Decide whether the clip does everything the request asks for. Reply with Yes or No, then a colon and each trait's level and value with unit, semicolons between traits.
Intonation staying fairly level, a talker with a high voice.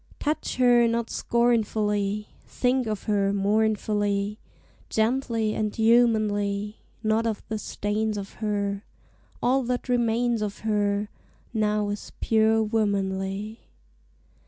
Yes: narrow, 1.9 semitones; high, 215 Hz